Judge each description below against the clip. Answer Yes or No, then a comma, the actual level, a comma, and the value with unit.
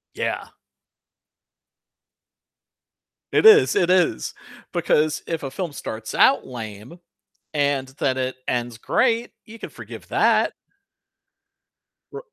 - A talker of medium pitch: Yes, medium, 145 Hz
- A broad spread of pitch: Yes, wide, 7.1 semitones